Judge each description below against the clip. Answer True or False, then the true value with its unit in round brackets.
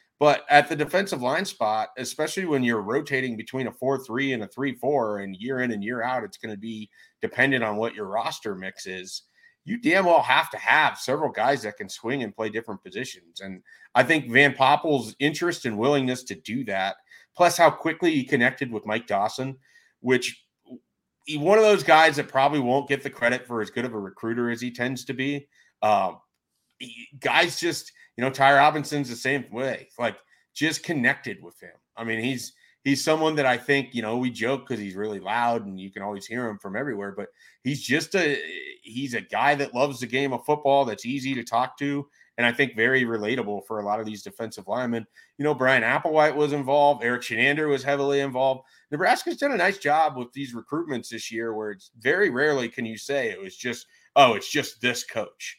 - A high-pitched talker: False (130 Hz)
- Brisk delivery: True (210 wpm)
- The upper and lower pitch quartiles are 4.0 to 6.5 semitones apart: True (4.3 semitones)